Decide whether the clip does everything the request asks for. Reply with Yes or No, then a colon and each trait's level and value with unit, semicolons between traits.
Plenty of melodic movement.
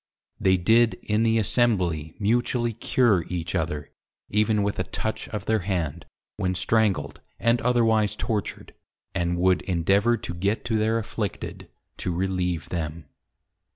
No: average, 4.3 semitones